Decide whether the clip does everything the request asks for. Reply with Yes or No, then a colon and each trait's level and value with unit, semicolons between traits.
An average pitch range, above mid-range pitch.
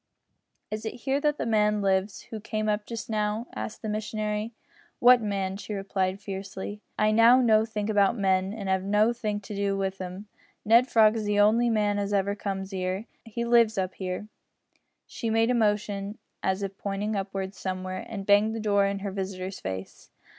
No: narrow, 2.0 semitones; high, 205 Hz